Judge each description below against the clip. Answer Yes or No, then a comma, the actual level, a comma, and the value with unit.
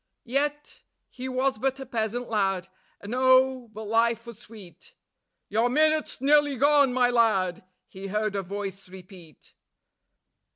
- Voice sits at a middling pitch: No, high, 230 Hz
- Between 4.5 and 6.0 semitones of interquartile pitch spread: Yes, average, 4.8 semitones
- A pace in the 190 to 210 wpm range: No, slow, 135 wpm